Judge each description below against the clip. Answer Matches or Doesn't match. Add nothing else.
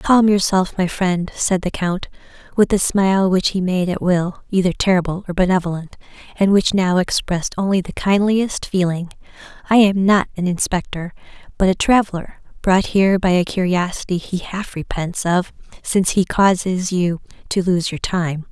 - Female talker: Matches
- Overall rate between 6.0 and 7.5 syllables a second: Doesn't match